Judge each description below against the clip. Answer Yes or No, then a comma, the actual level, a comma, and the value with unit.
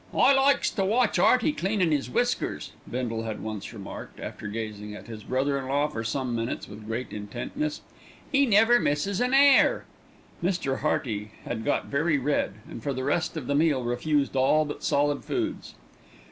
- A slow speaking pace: No, average, 175 wpm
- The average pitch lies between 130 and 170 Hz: Yes, medium, 140 Hz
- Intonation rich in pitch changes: Yes, wide, 8.2 semitones